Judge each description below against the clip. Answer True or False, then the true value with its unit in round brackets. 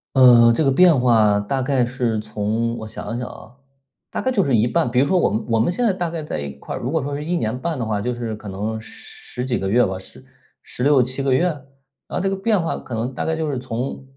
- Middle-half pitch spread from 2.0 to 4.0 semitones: False (4.5 semitones)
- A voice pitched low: True (125 Hz)